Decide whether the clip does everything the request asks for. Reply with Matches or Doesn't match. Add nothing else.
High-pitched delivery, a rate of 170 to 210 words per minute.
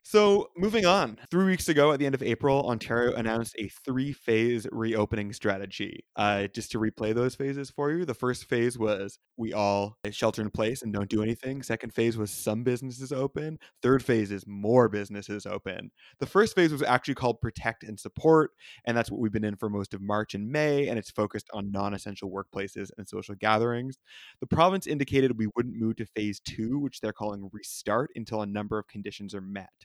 Doesn't match